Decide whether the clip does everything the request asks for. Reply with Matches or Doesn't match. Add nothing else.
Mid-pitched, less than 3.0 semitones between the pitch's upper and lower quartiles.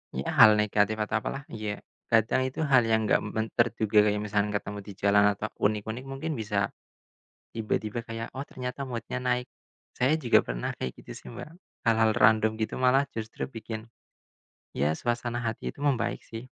Doesn't match